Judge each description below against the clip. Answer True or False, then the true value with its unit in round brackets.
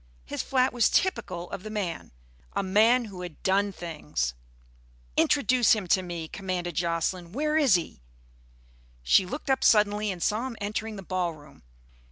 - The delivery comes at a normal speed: True (160 wpm)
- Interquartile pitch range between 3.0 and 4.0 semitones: False (4.4 semitones)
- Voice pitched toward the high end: True (195 Hz)